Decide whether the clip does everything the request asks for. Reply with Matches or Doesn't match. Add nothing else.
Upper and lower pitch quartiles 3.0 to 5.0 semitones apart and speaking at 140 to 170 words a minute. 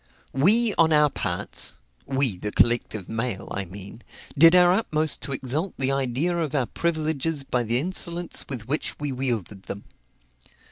Doesn't match